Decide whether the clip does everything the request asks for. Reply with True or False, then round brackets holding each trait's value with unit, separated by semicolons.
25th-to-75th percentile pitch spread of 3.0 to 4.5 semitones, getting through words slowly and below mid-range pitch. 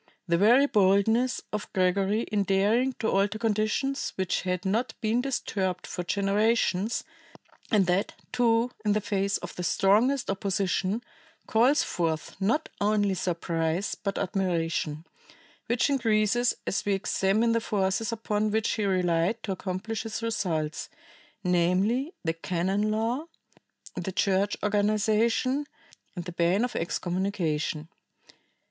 False (3.4 semitones; 125 wpm; 200 Hz)